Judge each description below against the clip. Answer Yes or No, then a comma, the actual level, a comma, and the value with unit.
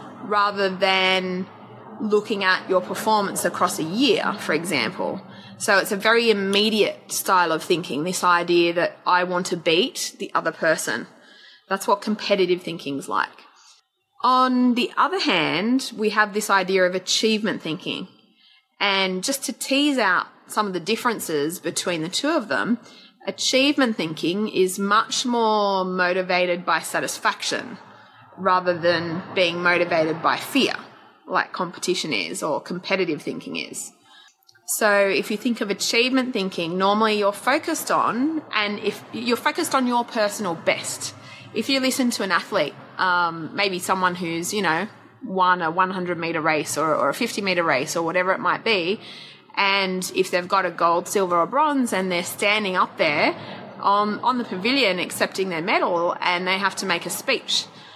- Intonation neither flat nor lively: Yes, average, 4.0 semitones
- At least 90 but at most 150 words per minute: No, average, 160 wpm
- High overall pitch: Yes, high, 195 Hz